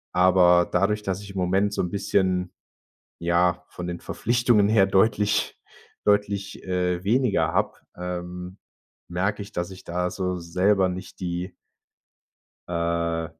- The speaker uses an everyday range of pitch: No, narrow, 2.3 semitones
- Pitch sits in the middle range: No, very low, 90 Hz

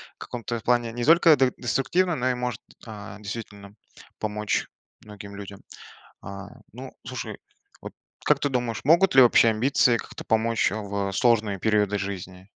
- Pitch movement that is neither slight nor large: Yes, average, 3.5 semitones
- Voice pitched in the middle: No, low, 110 Hz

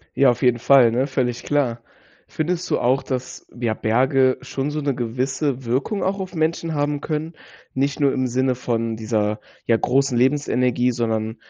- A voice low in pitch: Yes, low, 130 Hz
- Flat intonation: No, average, 3.2 semitones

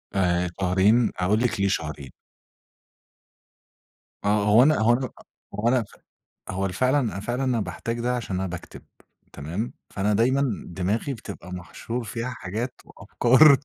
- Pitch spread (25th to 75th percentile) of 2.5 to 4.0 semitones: No, average, 4.5 semitones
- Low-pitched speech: Yes, low, 110 Hz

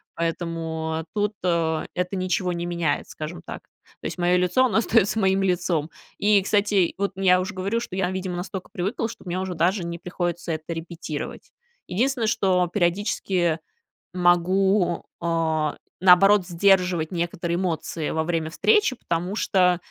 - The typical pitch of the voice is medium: Yes, medium, 180 Hz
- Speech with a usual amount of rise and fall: No, narrow, 2.3 semitones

